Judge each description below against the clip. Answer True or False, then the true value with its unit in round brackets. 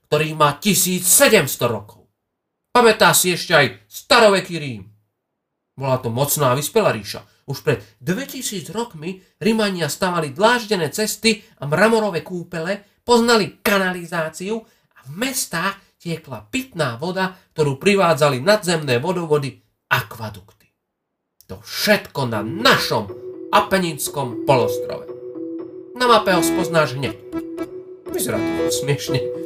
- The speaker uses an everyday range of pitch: False (7.1 semitones)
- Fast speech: False (110 wpm)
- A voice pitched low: False (170 Hz)